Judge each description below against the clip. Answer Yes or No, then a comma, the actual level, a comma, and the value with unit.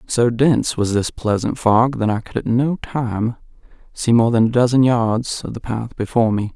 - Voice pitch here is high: No, low, 115 Hz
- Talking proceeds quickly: Yes, fast, 210 wpm